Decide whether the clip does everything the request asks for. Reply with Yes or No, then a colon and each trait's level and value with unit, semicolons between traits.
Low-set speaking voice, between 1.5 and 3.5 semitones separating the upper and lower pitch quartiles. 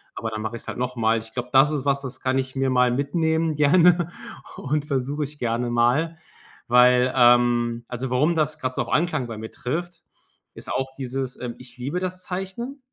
No: low, 130 Hz; average, 3.9 semitones